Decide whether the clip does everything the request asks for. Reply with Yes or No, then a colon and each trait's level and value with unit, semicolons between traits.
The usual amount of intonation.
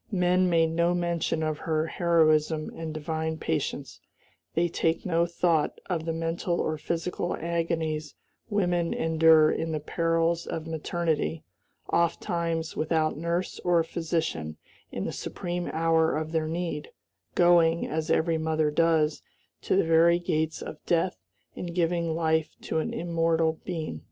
No: narrow, 1.3 semitones